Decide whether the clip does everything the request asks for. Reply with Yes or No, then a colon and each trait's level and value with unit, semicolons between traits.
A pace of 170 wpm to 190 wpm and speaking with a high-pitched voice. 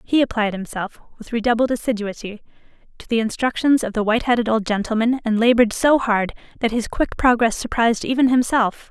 Yes: average, 175 wpm; high, 230 Hz